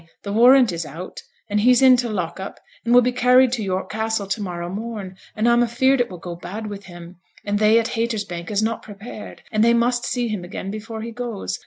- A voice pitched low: No, high, 215 Hz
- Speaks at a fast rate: Yes, fast, 230 wpm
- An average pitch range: Yes, average, 3.7 semitones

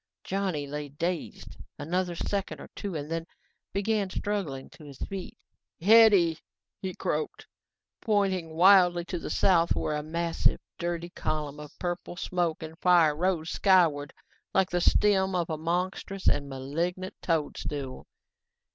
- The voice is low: No, medium, 175 Hz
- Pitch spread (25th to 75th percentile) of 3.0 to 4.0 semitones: Yes, average, 3.3 semitones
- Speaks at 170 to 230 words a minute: No, average, 140 wpm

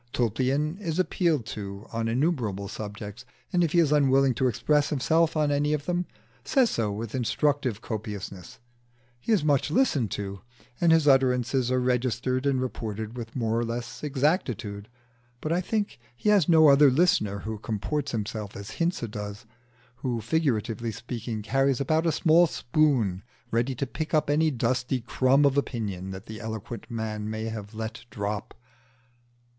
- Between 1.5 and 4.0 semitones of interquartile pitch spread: No, average, 5.2 semitones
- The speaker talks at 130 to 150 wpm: No, average, 165 wpm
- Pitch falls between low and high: No, low, 125 Hz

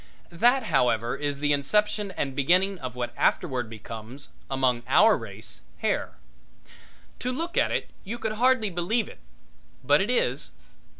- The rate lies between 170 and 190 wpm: No, average, 145 wpm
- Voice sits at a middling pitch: Yes, medium, 170 Hz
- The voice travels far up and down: Yes, wide, 8.6 semitones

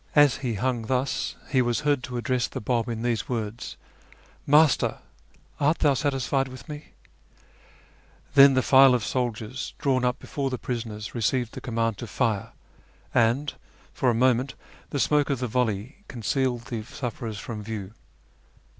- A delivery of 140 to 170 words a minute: Yes, average, 165 wpm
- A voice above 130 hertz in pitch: No, low, 125 Hz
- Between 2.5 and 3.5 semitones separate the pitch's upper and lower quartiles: Yes, average, 2.9 semitones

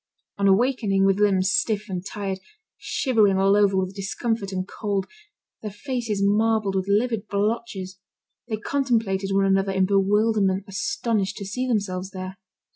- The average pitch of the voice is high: Yes, high, 200 Hz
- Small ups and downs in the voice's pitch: Yes, narrow, 2.3 semitones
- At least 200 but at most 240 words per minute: No, average, 145 wpm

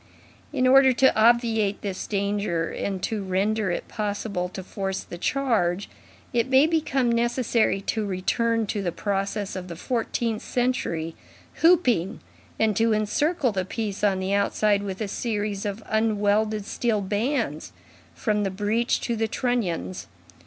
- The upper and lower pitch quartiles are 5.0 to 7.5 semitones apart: No, average, 3.2 semitones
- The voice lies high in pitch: Yes, high, 210 Hz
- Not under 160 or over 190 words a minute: No, average, 145 wpm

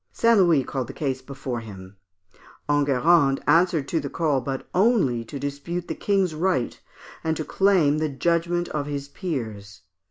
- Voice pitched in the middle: Yes, medium, 145 Hz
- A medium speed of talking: Yes, average, 160 wpm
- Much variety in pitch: No, average, 4.5 semitones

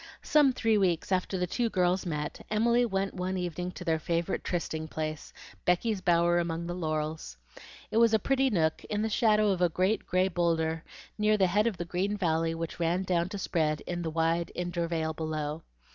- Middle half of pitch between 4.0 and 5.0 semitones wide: No, average, 3.3 semitones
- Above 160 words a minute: Yes, average, 195 wpm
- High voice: No, medium, 175 Hz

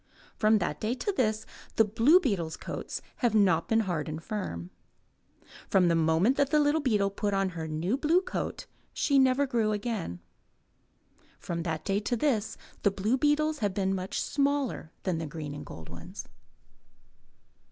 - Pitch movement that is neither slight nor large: No, wide, 7.3 semitones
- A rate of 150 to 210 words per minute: Yes, average, 170 wpm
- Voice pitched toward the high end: Yes, high, 210 Hz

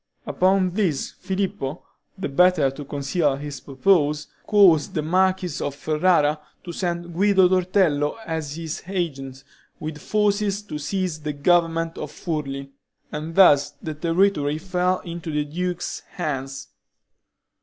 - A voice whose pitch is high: No, medium, 165 Hz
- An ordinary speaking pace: No, slow, 130 wpm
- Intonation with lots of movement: No, average, 3.9 semitones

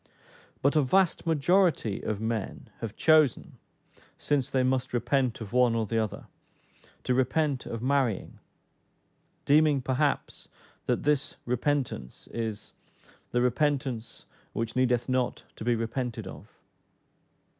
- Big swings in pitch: No, average, 3.7 semitones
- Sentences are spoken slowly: Yes, slow, 125 wpm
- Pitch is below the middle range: Yes, low, 125 Hz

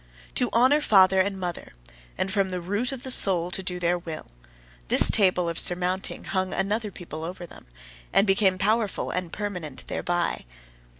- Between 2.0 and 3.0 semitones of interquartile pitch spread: Yes, narrow, 2.4 semitones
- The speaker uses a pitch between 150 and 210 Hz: Yes, medium, 185 Hz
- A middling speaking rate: Yes, average, 170 wpm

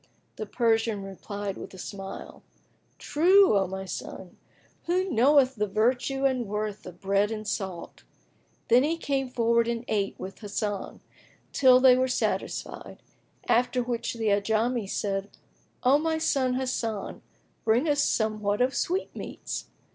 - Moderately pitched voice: No, high, 230 Hz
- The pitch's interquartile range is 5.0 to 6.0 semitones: No, average, 4.1 semitones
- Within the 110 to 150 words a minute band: Yes, average, 140 wpm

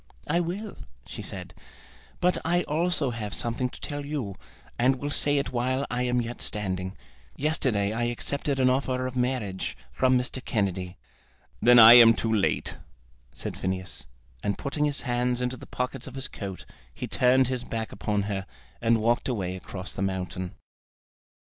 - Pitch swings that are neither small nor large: Yes, average, 4.5 semitones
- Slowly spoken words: No, average, 165 wpm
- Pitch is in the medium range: No, low, 125 Hz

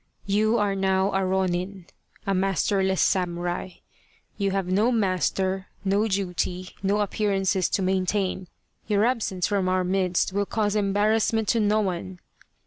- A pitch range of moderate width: No, narrow, 1.7 semitones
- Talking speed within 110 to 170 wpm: Yes, slow, 135 wpm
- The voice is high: Yes, high, 195 Hz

